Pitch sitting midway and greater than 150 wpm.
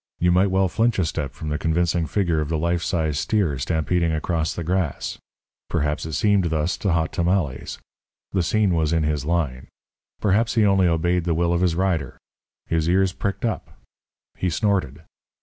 No: very low, 85 Hz; average, 185 wpm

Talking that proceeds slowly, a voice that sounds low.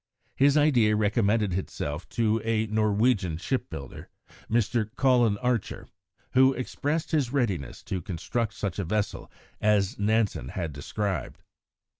Yes: slow, 125 wpm; low, 110 Hz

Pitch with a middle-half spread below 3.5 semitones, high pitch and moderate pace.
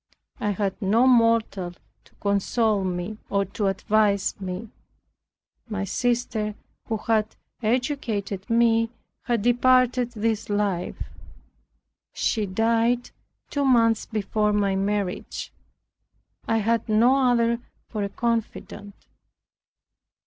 No: narrow, 2.5 semitones; high, 215 Hz; slow, 105 wpm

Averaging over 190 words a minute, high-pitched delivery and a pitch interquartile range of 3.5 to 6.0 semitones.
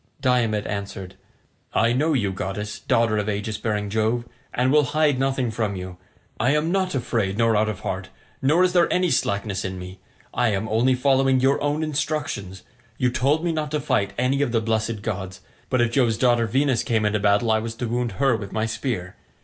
No: fast, 205 wpm; low, 115 Hz; average, 4.4 semitones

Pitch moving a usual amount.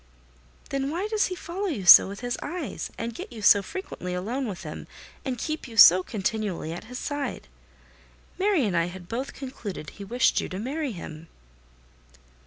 No: wide, 6.9 semitones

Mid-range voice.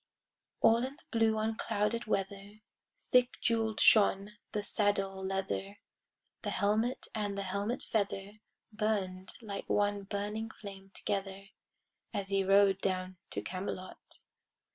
No: high, 200 Hz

